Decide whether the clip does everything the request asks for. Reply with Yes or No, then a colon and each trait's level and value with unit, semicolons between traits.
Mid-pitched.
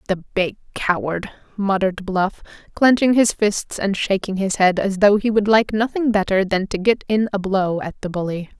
No: high, 200 Hz